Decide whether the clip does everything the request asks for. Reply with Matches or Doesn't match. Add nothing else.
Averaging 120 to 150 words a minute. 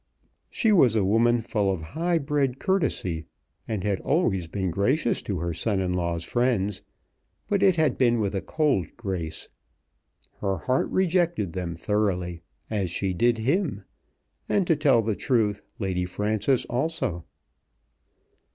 Matches